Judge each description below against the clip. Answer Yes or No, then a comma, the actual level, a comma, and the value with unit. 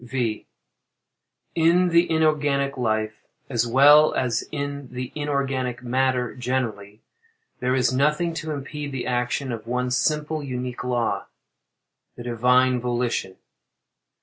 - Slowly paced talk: Yes, slow, 115 wpm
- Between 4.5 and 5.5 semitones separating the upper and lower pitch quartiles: No, average, 3.0 semitones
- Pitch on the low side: Yes, low, 130 Hz